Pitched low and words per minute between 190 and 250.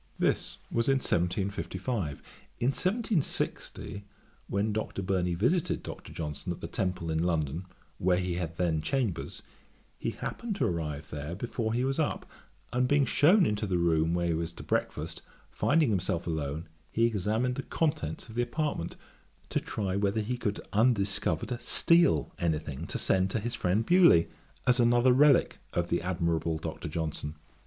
No: very low, 95 Hz; average, 165 wpm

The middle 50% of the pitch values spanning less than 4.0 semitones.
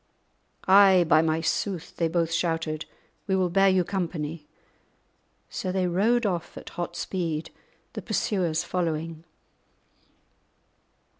Yes: narrow, 2.5 semitones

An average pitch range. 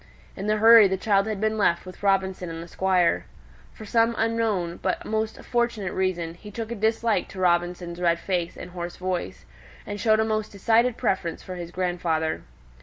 Yes: average, 3.8 semitones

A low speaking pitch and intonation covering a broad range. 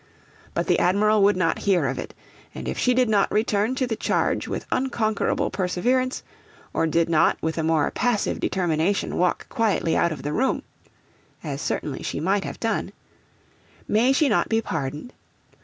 No: high, 200 Hz; wide, 5.7 semitones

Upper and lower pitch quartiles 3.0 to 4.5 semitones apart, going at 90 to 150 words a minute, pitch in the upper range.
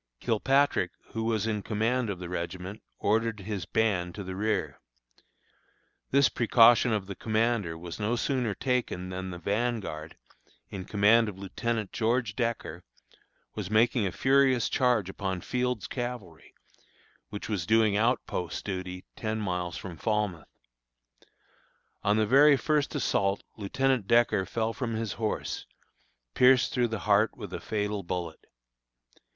No: average, 3.7 semitones; average, 140 wpm; low, 110 Hz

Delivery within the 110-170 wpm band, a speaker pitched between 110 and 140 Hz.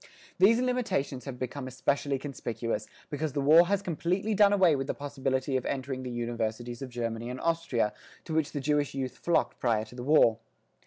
No: average, 190 wpm; low, 135 Hz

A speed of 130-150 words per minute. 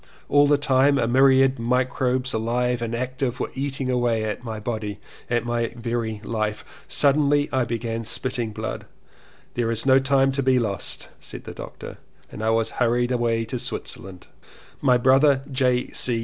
No: average, 165 wpm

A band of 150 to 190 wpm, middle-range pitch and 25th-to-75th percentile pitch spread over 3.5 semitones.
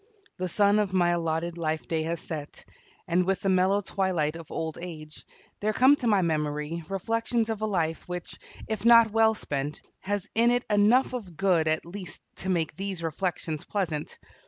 Yes: average, 180 wpm; medium, 180 Hz; average, 4.2 semitones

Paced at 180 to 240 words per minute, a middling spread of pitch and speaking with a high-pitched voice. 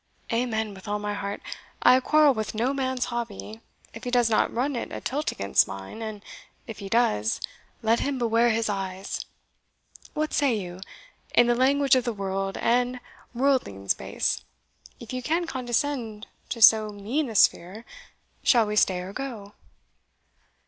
No: average, 165 wpm; average, 3.7 semitones; high, 230 Hz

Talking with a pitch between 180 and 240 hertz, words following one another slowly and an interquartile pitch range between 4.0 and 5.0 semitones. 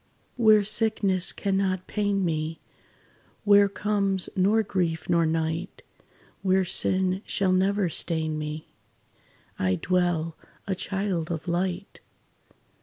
No: medium, 185 Hz; slow, 110 wpm; average, 3.1 semitones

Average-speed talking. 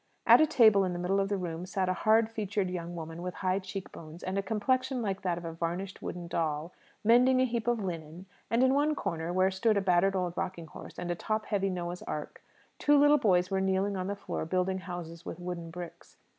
No: fast, 235 wpm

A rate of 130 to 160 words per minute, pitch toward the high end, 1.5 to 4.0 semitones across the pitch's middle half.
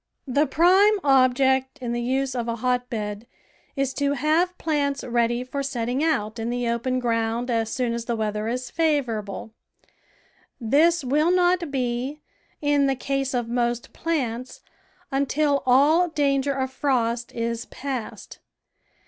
Yes: average, 150 wpm; very high, 255 Hz; average, 3.3 semitones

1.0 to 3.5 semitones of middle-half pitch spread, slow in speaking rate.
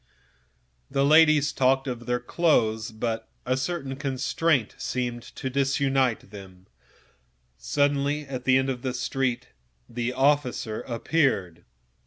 Yes: average, 2.8 semitones; slow, 120 wpm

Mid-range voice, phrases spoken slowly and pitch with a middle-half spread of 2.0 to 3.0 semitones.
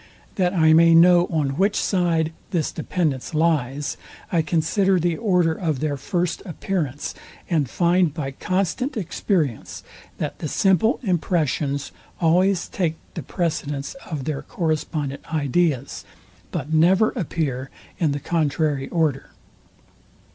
No: medium, 160 Hz; slow, 125 wpm; average, 3.4 semitones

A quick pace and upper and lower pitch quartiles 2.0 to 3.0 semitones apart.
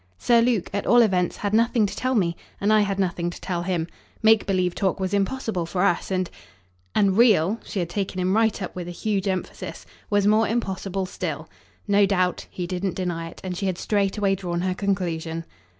Yes: fast, 210 wpm; narrow, 2.5 semitones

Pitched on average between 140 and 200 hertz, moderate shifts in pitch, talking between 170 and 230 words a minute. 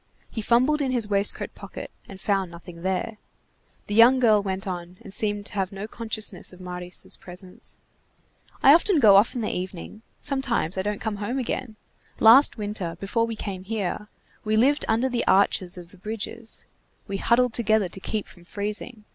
No: high, 210 Hz; average, 3.4 semitones; average, 180 wpm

